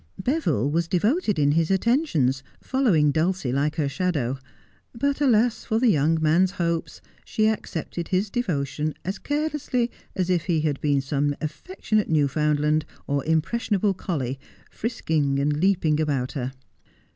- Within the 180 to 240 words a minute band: No, average, 140 wpm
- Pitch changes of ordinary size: No, wide, 6.6 semitones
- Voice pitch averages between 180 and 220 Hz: No, medium, 165 Hz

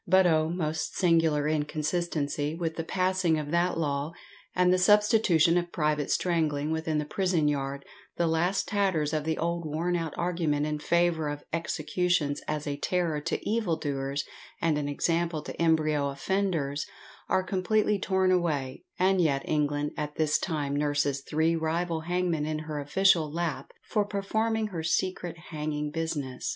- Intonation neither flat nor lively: Yes, average, 3.1 semitones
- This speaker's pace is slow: No, average, 160 wpm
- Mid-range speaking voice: Yes, medium, 160 Hz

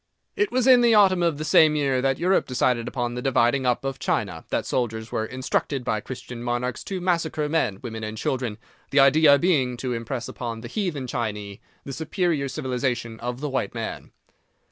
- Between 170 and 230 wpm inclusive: Yes, average, 190 wpm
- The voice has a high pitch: No, low, 130 Hz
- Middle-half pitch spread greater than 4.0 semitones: Yes, average, 4.5 semitones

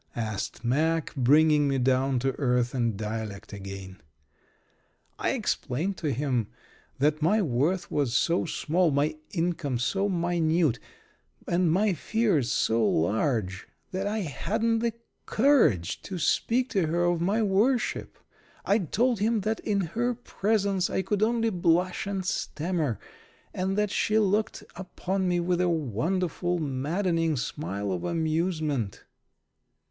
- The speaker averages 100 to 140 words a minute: Yes, slow, 135 wpm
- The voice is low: No, medium, 170 Hz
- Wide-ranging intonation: Yes, wide, 6.6 semitones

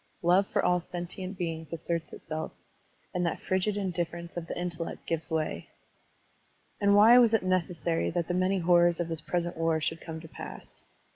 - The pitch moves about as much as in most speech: No, narrow, 2.0 semitones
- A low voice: No, medium, 175 Hz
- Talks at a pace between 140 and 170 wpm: No, average, 180 wpm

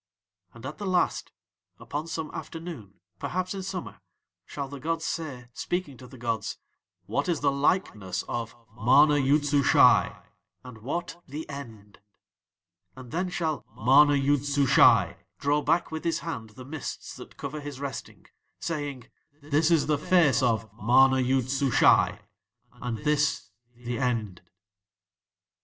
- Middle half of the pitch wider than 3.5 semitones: Yes, average, 4.1 semitones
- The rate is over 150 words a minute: No, average, 140 wpm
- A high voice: No, medium, 140 Hz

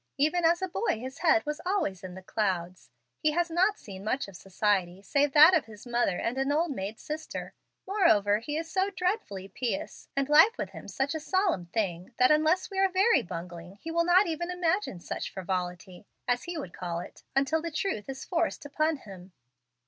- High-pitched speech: Yes, very high, 280 Hz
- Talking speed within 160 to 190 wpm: No, average, 200 wpm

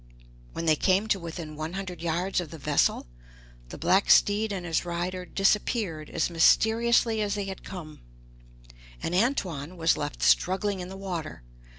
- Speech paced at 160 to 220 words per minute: Yes, average, 165 wpm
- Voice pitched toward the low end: No, medium, 180 Hz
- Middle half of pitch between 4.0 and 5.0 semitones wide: No, average, 3.2 semitones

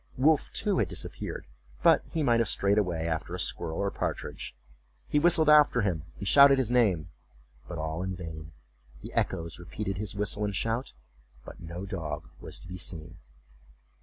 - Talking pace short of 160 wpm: No, average, 175 wpm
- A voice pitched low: Yes, very low, 95 Hz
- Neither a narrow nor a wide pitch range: No, wide, 6.0 semitones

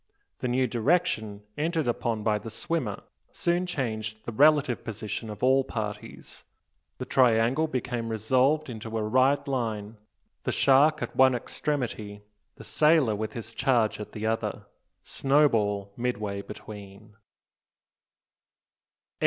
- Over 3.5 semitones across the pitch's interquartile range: Yes, average, 4.0 semitones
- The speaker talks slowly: Yes, slow, 125 wpm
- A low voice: Yes, low, 115 Hz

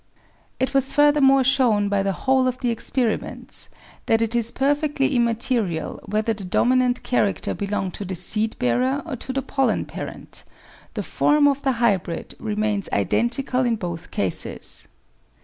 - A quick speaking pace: No, average, 150 wpm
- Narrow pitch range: No, average, 4.6 semitones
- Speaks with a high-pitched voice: Yes, high, 235 Hz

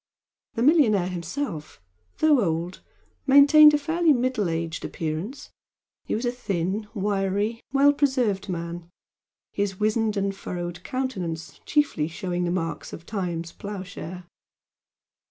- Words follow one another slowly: Yes, slow, 120 wpm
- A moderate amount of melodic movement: No, wide, 6.7 semitones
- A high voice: Yes, high, 200 Hz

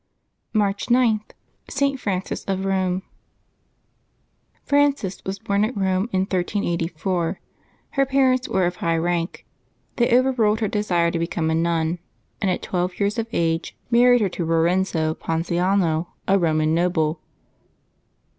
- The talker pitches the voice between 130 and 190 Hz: Yes, medium, 185 Hz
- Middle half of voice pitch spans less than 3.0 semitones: No, average, 4.0 semitones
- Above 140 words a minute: No, slow, 135 wpm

